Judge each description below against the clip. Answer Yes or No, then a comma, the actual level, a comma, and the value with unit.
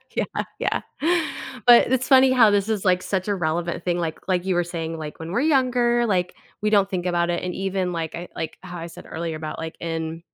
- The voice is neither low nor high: Yes, medium, 180 Hz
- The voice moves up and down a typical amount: Yes, average, 3.8 semitones